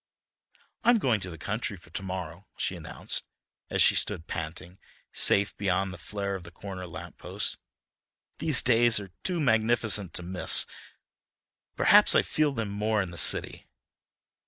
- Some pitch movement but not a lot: Yes, average, 3.9 semitones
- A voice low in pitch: Yes, low, 100 Hz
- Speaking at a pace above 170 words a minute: No, average, 160 wpm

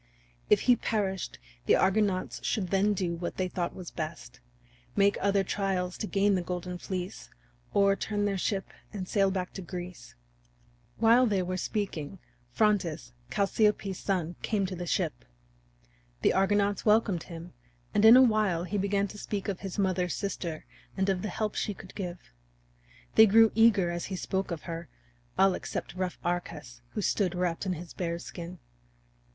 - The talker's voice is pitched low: No, high, 190 Hz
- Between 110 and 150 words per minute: No, average, 170 wpm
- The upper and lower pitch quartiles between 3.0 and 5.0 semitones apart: No, narrow, 2.5 semitones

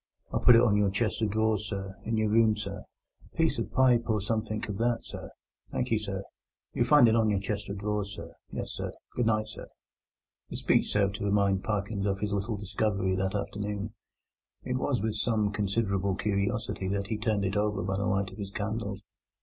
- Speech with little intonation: Yes, narrow, 1.9 semitones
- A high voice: No, low, 105 Hz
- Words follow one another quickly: Yes, fast, 210 wpm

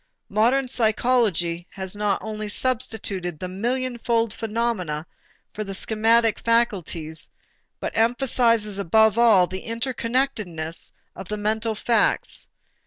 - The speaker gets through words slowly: Yes, slow, 105 wpm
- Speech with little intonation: No, average, 3.6 semitones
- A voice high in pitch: Yes, high, 220 Hz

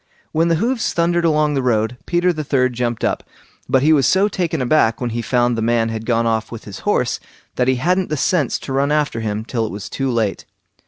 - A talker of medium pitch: No, low, 130 Hz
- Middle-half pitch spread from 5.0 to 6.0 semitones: Yes, wide, 5.4 semitones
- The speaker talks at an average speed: No, fast, 235 wpm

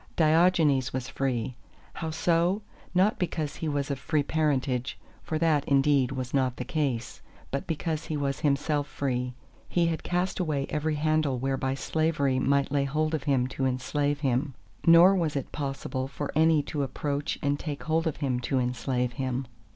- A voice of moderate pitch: Yes, medium, 145 Hz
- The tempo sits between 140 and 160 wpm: No, average, 175 wpm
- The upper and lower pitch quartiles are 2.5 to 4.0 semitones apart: Yes, average, 2.9 semitones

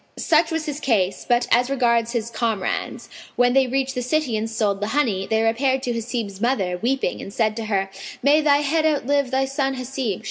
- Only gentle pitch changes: No, average, 3.6 semitones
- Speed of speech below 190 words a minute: No, fast, 205 wpm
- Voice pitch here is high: Yes, high, 245 Hz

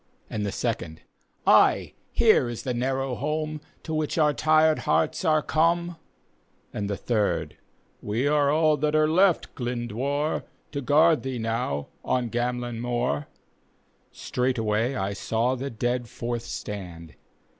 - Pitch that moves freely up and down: No, average, 4.7 semitones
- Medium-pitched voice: No, low, 125 Hz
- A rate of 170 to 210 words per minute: No, average, 145 wpm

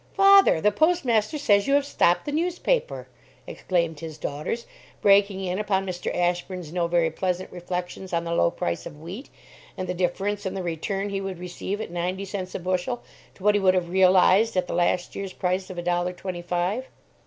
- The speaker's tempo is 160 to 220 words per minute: Yes, average, 200 wpm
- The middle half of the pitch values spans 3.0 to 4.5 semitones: No, narrow, 2.6 semitones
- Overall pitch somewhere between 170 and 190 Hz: Yes, medium, 185 Hz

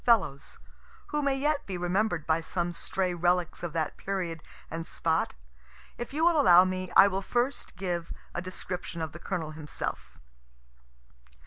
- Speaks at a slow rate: No, average, 155 wpm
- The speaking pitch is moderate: Yes, medium, 180 Hz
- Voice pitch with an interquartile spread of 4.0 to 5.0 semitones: No, average, 3.2 semitones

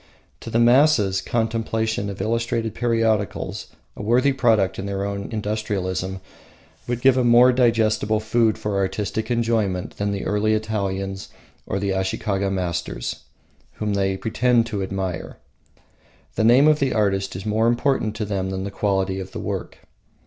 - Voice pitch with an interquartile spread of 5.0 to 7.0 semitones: No, average, 3.0 semitones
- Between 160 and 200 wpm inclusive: No, average, 150 wpm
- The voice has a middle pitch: No, low, 105 Hz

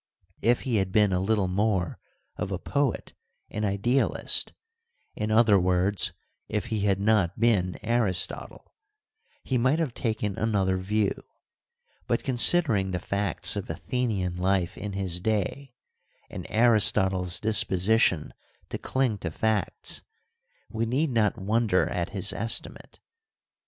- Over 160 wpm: No, slow, 135 wpm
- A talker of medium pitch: No, low, 105 Hz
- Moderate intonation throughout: Yes, average, 3.4 semitones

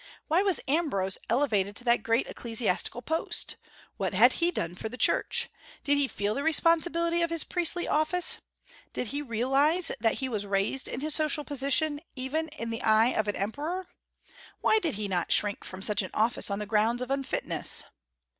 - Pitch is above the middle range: Yes, very high, 265 Hz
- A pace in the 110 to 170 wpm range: No, average, 185 wpm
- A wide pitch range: Yes, wide, 6.5 semitones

